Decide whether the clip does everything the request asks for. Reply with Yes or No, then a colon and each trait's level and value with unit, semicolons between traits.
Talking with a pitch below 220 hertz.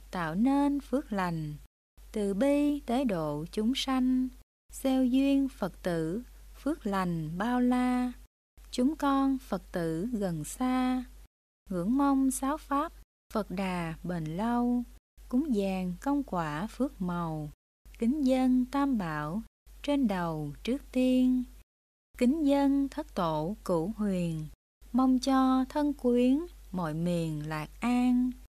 No: high, 245 Hz